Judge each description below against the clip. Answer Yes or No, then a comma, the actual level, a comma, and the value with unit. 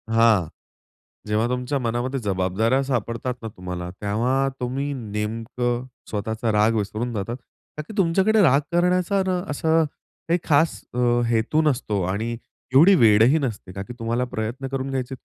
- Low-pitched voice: Yes, low, 120 Hz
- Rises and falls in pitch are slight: No, average, 4.2 semitones